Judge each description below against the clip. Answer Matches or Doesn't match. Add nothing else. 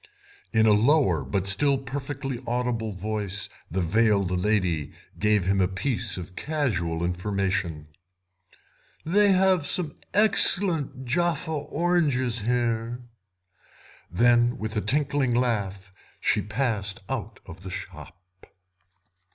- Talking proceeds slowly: Matches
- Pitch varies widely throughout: Matches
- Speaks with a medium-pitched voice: Doesn't match